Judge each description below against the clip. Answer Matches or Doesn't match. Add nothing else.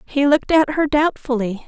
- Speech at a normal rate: Matches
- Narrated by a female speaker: Matches